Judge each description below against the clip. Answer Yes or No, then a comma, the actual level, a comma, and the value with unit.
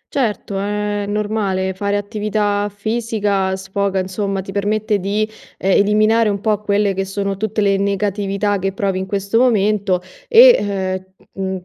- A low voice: No, high, 200 Hz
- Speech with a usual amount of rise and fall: No, narrow, 1.5 semitones